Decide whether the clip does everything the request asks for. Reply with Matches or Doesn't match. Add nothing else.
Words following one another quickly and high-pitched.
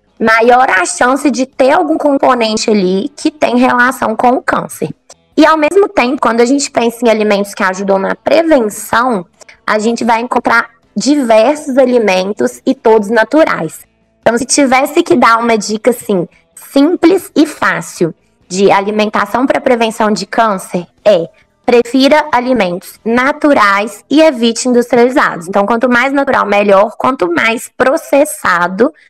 Doesn't match